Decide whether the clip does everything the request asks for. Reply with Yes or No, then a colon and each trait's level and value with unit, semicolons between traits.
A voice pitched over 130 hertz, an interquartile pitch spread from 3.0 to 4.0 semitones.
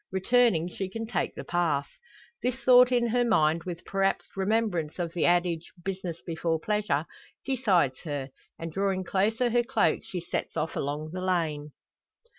No: medium, 185 Hz; average, 5.2 semitones